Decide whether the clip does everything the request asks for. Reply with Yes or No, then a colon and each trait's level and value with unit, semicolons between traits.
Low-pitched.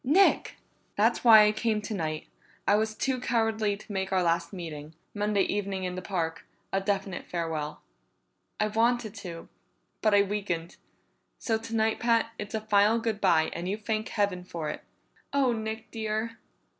No: high, 210 Hz